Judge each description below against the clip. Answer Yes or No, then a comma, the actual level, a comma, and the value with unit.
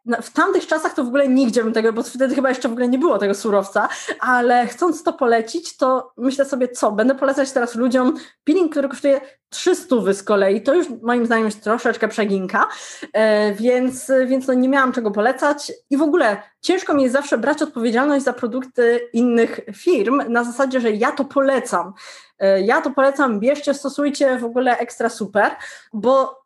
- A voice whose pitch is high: Yes, very high, 255 Hz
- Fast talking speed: Yes, fast, 180 wpm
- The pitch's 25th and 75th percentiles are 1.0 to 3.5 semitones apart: Yes, average, 3.2 semitones